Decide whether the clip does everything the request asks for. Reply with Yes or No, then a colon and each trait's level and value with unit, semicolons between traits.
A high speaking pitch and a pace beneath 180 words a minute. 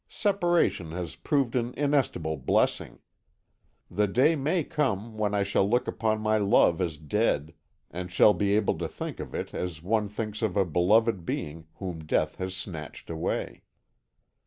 No: low, 105 Hz; average, 160 wpm